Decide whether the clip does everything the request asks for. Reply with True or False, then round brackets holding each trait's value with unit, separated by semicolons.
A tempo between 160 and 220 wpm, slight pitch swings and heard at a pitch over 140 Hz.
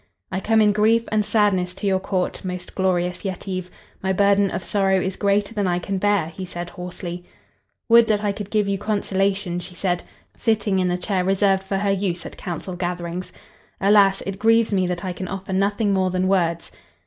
True (200 wpm; 2.0 semitones; 190 Hz)